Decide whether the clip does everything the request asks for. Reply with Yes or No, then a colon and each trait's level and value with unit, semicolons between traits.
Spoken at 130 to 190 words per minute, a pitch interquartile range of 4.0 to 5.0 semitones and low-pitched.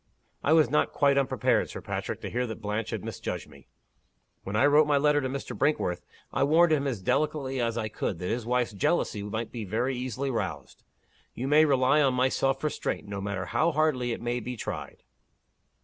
No: fast, 205 wpm; average, 4.4 semitones; low, 130 Hz